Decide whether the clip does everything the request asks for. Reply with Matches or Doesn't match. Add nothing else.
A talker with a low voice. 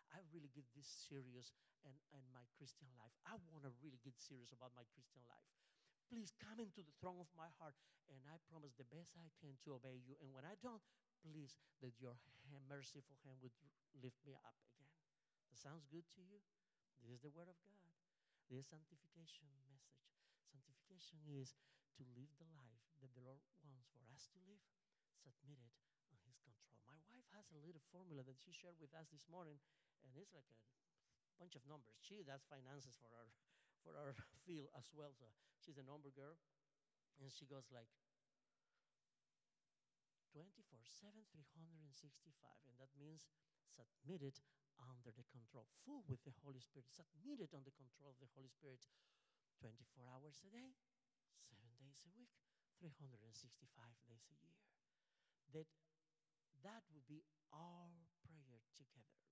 Doesn't match